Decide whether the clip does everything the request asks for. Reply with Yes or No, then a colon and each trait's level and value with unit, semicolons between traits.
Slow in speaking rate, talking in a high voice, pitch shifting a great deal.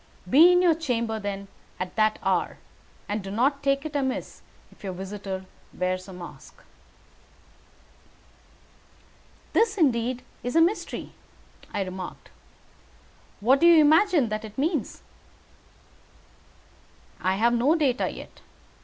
Yes: slow, 125 wpm; high, 240 Hz; wide, 7.4 semitones